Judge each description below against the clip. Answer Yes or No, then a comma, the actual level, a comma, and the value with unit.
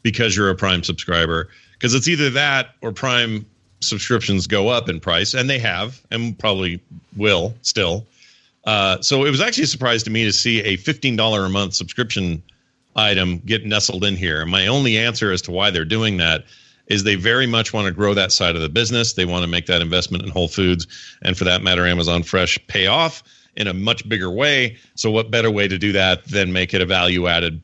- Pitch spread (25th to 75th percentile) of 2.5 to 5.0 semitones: Yes, average, 4.3 semitones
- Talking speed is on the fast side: Yes, fast, 220 wpm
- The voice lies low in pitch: Yes, low, 100 Hz